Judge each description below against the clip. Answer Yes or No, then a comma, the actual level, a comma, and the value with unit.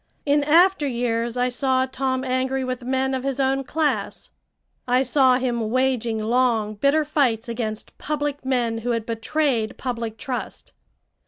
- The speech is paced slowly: No, average, 150 wpm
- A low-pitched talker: No, very high, 255 Hz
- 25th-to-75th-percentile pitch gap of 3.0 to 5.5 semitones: No, narrow, 2.6 semitones